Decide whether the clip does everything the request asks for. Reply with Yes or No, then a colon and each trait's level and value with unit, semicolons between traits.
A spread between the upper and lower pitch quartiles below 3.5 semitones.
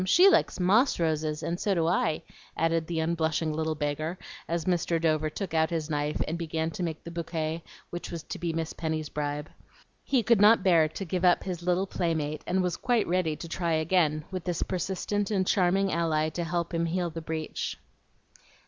Yes: narrow, 2.4 semitones